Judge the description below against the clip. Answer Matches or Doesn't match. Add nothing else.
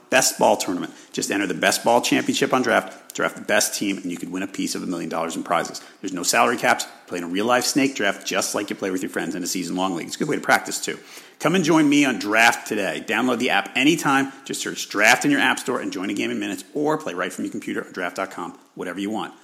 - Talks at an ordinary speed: Doesn't match